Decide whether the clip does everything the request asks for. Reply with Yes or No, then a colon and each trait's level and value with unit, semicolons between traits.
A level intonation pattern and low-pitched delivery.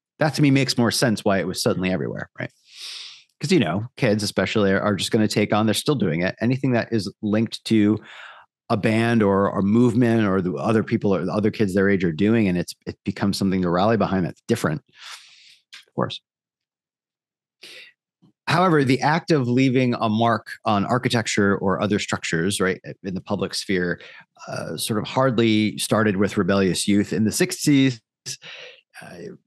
No: average, 3.4 semitones; low, 110 Hz